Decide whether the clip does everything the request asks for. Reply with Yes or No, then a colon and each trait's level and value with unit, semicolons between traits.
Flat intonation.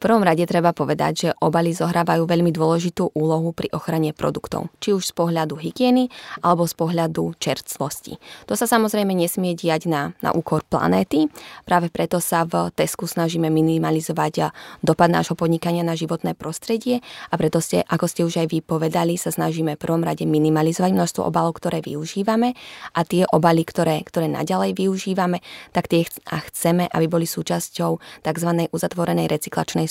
Yes: narrow, 1.6 semitones